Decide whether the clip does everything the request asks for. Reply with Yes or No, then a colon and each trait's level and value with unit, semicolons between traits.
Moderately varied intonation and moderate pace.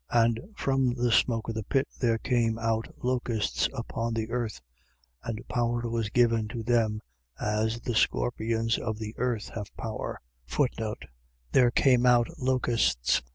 No: narrow, 1.6 semitones; average, 150 wpm